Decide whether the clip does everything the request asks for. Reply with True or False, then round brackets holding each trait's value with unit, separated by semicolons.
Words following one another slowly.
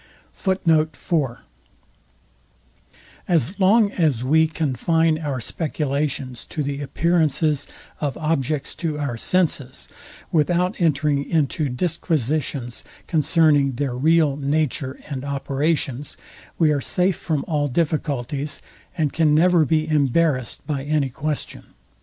True (105 wpm)